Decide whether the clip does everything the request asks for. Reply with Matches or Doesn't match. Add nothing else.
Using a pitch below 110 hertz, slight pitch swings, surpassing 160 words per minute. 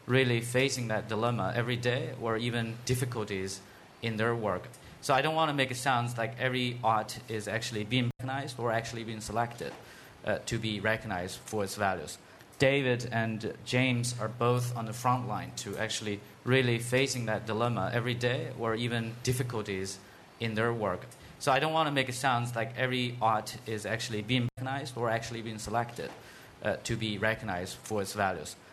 Doesn't match